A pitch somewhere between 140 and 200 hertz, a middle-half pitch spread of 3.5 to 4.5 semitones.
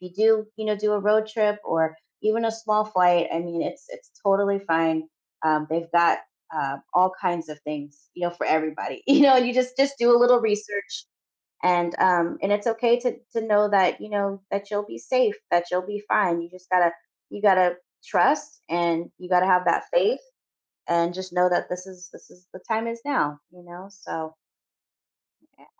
Yes: high, 190 Hz; average, 3.8 semitones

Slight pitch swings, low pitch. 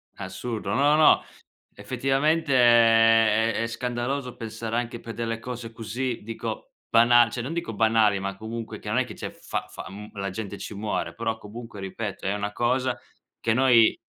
Yes: narrow, 2.1 semitones; low, 115 Hz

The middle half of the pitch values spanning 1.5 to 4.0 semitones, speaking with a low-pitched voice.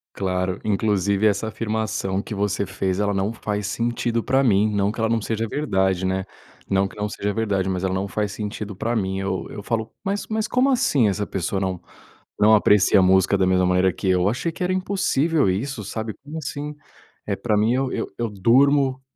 Yes: average, 3.5 semitones; low, 105 Hz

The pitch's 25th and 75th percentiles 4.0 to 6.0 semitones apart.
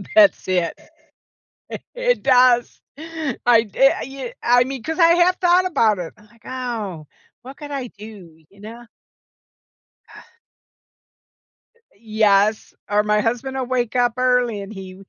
Yes: average, 4.4 semitones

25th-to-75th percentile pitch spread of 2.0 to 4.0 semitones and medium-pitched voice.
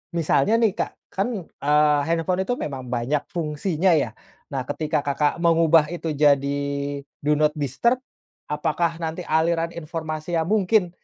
Yes: average, 2.7 semitones; medium, 160 Hz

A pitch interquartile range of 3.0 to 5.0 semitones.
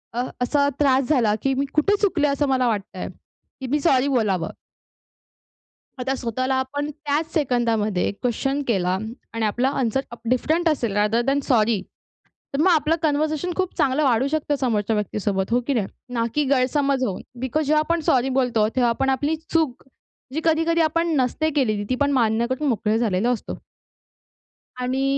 Yes: average, 4.2 semitones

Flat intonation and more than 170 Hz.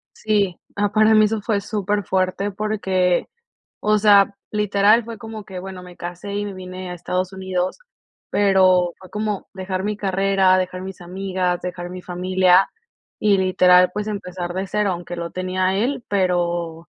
Yes: narrow, 2.1 semitones; high, 190 Hz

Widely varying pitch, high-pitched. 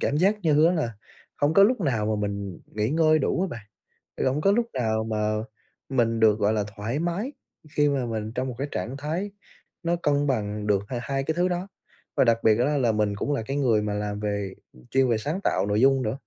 No: wide, 6.0 semitones; low, 125 Hz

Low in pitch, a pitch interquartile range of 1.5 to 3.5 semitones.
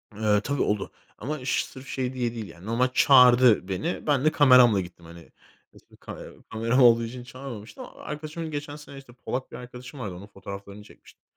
No: low, 125 Hz; average, 4.4 semitones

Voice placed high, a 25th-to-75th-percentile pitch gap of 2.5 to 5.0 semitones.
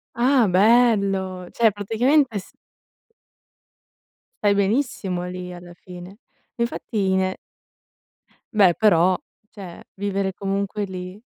Yes: high, 195 Hz; average, 2.9 semitones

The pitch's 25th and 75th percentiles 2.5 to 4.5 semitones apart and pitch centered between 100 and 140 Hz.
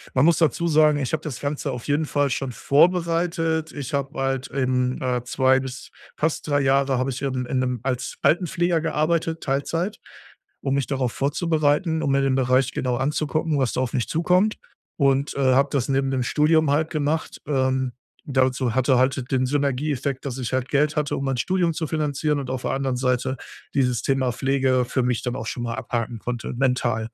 Yes: average, 2.9 semitones; low, 135 Hz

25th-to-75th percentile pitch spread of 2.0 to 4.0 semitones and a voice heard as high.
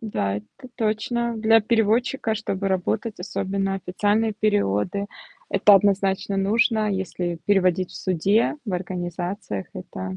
Yes: average, 3.2 semitones; high, 200 Hz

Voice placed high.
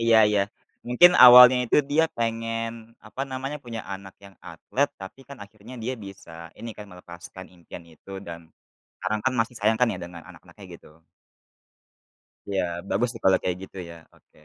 No: low, 110 Hz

